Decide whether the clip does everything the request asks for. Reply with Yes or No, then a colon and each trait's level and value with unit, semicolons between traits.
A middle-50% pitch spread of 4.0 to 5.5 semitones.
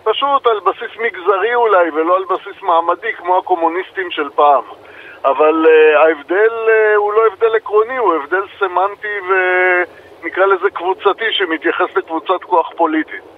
Yes: average, 4.3 semitones